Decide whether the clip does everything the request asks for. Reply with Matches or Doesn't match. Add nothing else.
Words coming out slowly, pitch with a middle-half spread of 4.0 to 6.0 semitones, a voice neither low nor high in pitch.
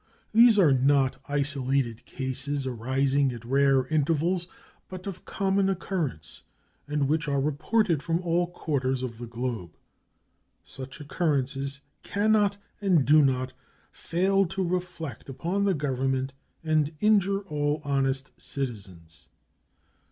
Matches